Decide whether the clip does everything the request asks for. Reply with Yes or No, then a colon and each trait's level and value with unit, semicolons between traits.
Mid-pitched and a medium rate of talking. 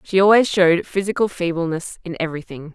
Yes: medium, 175 Hz; average, 155 wpm